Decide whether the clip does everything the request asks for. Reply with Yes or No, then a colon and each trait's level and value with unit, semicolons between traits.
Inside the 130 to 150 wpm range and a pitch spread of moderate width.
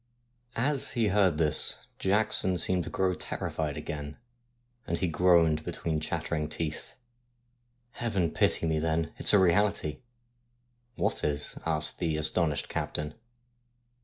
No: average, 140 wpm; wide, 6.0 semitones